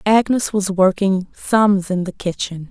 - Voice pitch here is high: Yes, high, 195 Hz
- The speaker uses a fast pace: No, average, 155 wpm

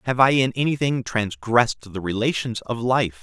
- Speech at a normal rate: Yes, average, 165 wpm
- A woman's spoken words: No, male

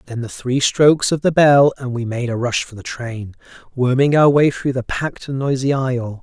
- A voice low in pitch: Yes, low, 130 Hz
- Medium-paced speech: No, fast, 230 wpm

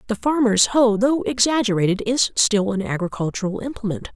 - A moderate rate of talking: Yes, average, 145 wpm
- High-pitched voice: Yes, high, 220 Hz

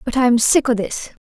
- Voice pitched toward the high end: Yes, high, 245 Hz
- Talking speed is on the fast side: Yes, fast, 240 wpm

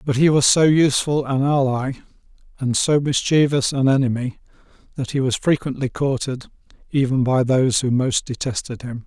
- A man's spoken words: Yes, male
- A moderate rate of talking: Yes, average, 160 wpm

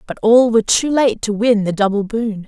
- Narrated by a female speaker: Yes, female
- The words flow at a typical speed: No, fast, 245 wpm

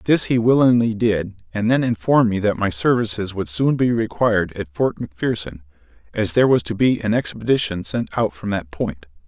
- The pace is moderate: Yes, average, 195 wpm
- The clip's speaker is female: No, male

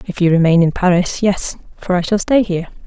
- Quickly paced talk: Yes, fast, 230 wpm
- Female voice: Yes, female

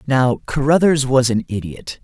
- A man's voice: Yes, male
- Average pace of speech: Yes, average, 145 wpm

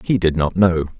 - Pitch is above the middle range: No, very low, 90 Hz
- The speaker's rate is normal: No, fast, 240 wpm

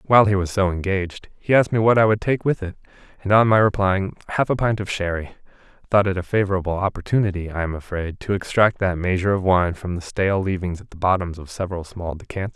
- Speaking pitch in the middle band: No, very low, 95 Hz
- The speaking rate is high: Yes, fast, 225 wpm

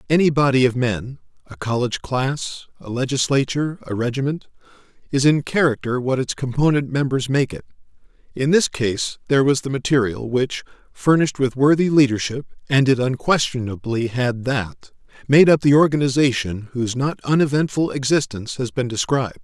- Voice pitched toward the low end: Yes, low, 130 Hz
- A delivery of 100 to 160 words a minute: Yes, slow, 135 wpm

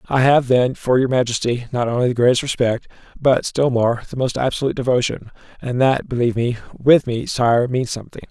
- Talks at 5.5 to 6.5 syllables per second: Yes, 5.7 syllables/s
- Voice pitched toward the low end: Yes, low, 125 Hz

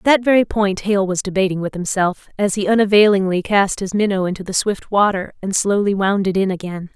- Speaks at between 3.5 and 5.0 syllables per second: No, 5.5 syllables/s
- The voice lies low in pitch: No, high, 195 Hz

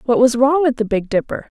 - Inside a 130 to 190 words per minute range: No, fast, 265 wpm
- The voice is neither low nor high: No, very high, 250 Hz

